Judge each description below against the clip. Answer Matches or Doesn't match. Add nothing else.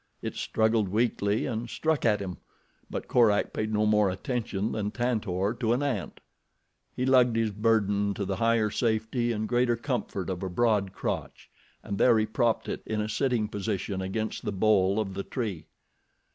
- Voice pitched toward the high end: Doesn't match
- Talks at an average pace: Matches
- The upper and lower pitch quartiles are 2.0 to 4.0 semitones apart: Matches